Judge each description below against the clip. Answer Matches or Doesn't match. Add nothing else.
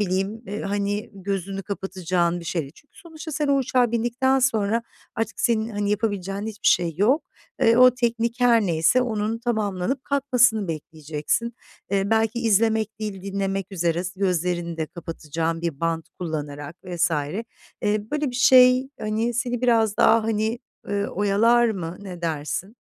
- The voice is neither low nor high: Doesn't match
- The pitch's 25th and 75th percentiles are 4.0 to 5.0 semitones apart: Matches